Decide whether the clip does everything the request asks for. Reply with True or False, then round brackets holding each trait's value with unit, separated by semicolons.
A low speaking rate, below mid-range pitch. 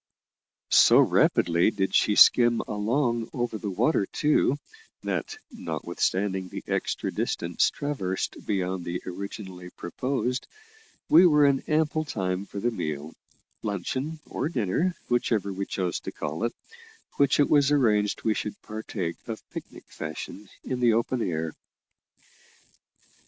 True (130 wpm; 110 Hz)